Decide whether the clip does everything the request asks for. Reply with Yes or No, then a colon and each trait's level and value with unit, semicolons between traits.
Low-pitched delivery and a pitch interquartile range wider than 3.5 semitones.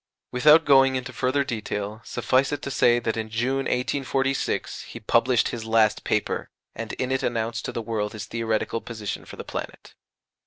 No: low, 120 Hz; average, 3.0 semitones